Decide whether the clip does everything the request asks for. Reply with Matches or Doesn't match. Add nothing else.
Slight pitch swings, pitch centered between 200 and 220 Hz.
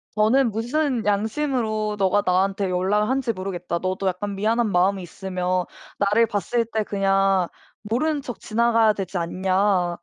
Doesn't match